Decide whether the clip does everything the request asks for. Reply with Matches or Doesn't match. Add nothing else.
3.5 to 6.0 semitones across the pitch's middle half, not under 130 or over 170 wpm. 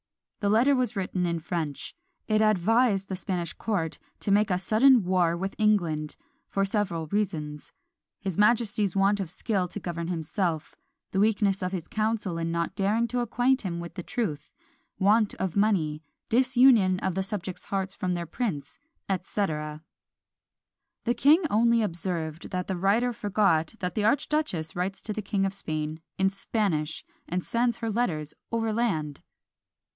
Matches